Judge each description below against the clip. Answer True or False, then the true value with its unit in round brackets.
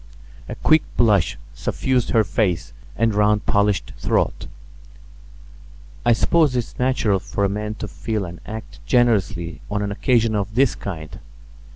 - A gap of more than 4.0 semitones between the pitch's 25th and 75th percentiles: False (2.8 semitones)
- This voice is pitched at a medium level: False (105 Hz)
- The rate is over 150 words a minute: False (145 wpm)